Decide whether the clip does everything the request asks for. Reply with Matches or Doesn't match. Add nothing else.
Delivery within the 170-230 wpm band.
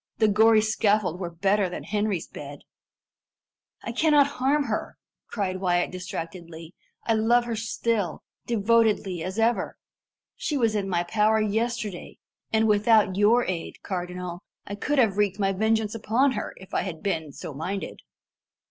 Doesn't match